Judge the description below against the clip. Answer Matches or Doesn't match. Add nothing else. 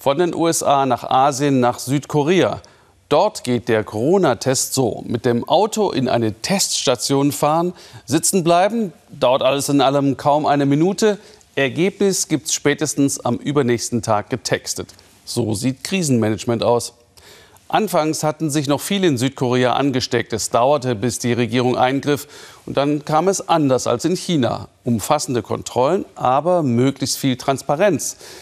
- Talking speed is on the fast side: Doesn't match